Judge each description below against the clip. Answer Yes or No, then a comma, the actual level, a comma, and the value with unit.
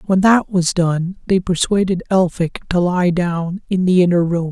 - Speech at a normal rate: Yes, average, 185 wpm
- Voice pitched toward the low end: No, medium, 180 Hz